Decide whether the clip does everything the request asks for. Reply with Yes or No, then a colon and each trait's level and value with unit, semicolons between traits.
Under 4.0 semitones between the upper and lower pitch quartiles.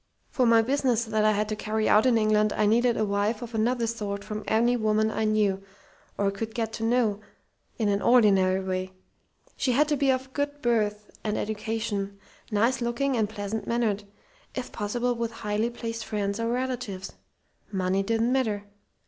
Yes: narrow, 2.4 semitones